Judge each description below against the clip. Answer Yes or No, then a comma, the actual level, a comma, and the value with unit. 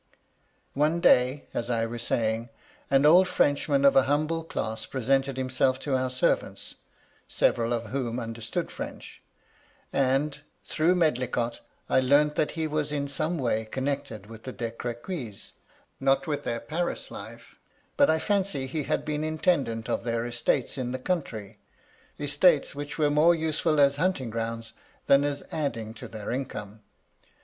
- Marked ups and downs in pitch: No, average, 4.2 semitones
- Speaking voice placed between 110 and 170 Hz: Yes, low, 135 Hz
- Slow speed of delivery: No, average, 155 wpm